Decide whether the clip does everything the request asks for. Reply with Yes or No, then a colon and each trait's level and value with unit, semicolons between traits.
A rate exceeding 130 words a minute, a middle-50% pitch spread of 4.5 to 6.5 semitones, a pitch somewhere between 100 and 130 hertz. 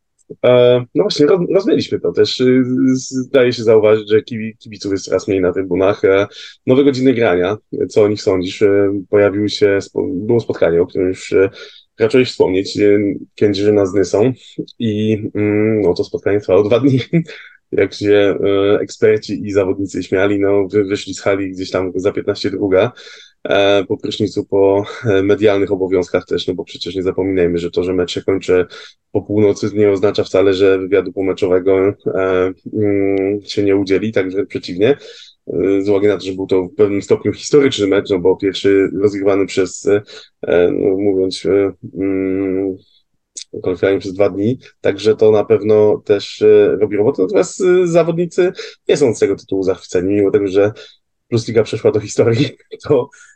Yes: average, 155 wpm; average, 5.2 semitones; low, 105 Hz